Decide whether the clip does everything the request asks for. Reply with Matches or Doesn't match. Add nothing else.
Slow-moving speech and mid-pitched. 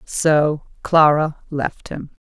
Matches